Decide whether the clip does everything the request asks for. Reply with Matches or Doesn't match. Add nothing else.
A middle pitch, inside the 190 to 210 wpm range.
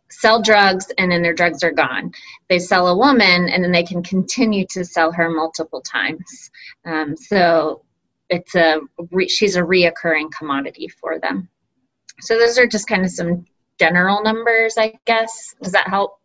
Doesn't match